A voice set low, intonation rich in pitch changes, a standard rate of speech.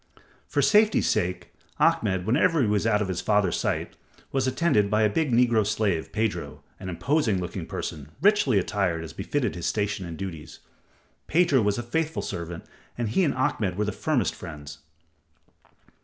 Yes: low, 105 Hz; wide, 6.2 semitones; average, 170 wpm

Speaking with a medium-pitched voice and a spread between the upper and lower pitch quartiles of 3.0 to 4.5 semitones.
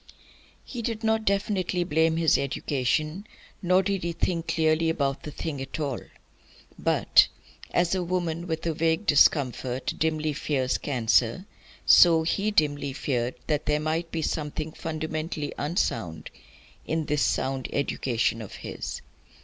Yes: medium, 155 Hz; average, 3.3 semitones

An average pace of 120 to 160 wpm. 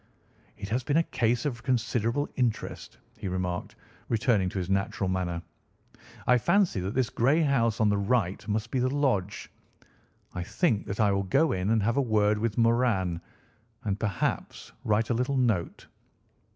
No: average, 170 wpm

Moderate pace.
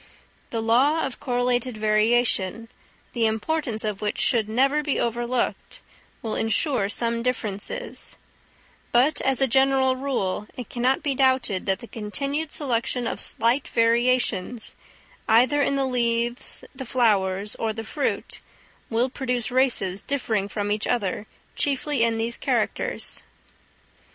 No: slow, 130 wpm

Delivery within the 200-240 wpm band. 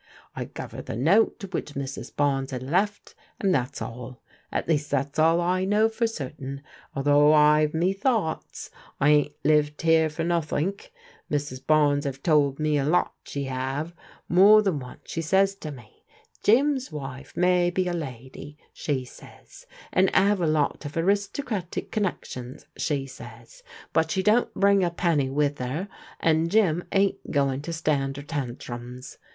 No: average, 165 wpm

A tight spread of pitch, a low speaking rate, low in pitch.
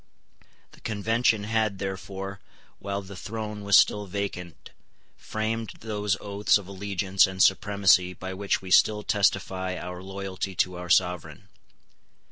Yes: narrow, 1.7 semitones; slow, 130 wpm; low, 100 Hz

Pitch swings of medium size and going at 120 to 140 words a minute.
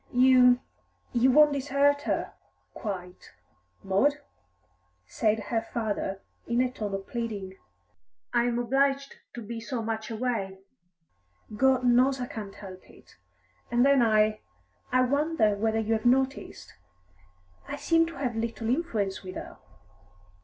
Yes: average, 3.5 semitones; slow, 135 wpm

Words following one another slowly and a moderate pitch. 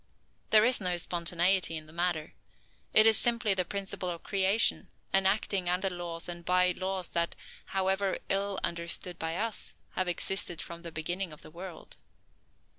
No: average, 165 wpm; medium, 180 Hz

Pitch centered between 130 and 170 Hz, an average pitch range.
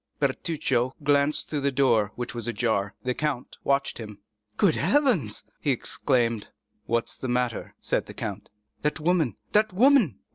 Yes: low, 135 Hz; average, 4.5 semitones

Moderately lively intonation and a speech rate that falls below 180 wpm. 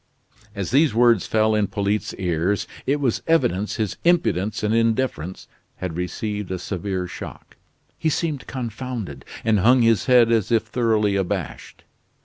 Yes: average, 4.0 semitones; average, 145 wpm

